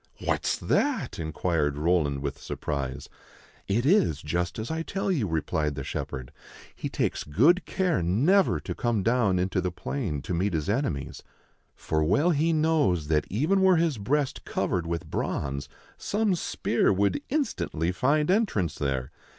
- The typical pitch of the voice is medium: No, very low, 95 Hz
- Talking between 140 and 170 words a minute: Yes, average, 160 wpm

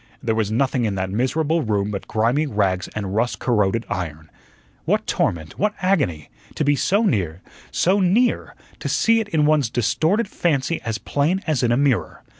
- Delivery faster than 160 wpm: Yes, average, 180 wpm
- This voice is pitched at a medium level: No, low, 125 Hz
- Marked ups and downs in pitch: Yes, wide, 7.7 semitones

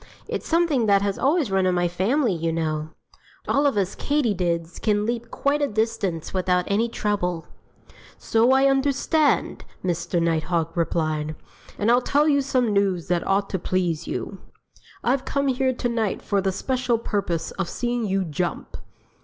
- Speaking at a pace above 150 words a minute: Yes, average, 165 wpm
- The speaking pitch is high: Yes, high, 200 Hz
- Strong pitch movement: Yes, wide, 6.3 semitones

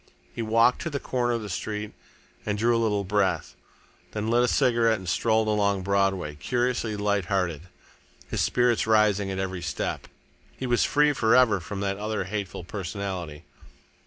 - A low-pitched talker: Yes, low, 105 Hz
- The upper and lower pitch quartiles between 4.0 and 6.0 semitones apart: No, average, 3.0 semitones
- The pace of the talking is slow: No, average, 175 wpm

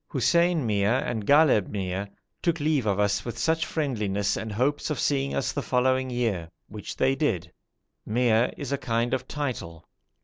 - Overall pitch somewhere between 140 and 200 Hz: No, low, 125 Hz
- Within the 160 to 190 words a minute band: Yes, average, 170 wpm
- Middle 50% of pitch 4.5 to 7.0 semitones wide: Yes, wide, 5.5 semitones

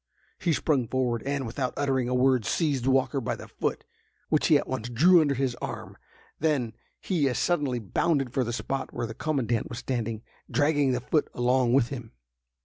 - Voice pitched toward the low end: Yes, low, 130 Hz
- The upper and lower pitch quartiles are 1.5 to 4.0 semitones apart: Yes, average, 3.0 semitones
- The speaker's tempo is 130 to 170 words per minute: No, average, 190 wpm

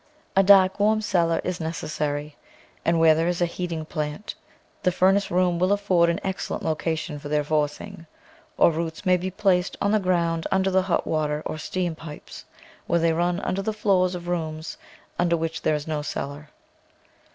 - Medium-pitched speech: Yes, medium, 170 Hz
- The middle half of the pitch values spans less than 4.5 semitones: Yes, average, 2.9 semitones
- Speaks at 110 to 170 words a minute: No, average, 185 wpm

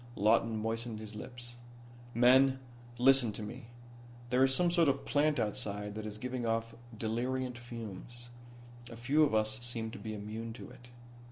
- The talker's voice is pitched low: Yes, low, 120 Hz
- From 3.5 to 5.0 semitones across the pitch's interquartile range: No, average, 2.7 semitones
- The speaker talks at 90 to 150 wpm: No, average, 165 wpm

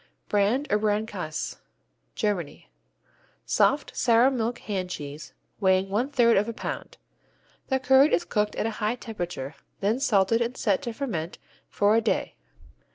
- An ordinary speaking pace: Yes, average, 150 wpm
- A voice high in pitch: Yes, high, 215 Hz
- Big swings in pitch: No, average, 3.7 semitones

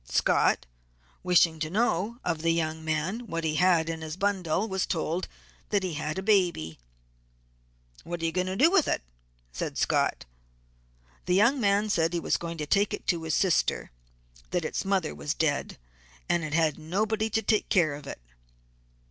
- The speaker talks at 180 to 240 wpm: Yes, average, 185 wpm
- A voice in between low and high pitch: Yes, medium, 170 Hz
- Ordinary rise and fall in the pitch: Yes, average, 3.8 semitones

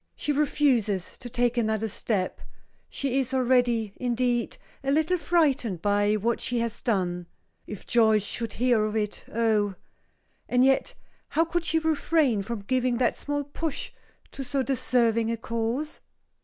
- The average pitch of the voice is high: Yes, high, 240 Hz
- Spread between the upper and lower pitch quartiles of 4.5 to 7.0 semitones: No, average, 3.7 semitones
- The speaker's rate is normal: Yes, average, 150 wpm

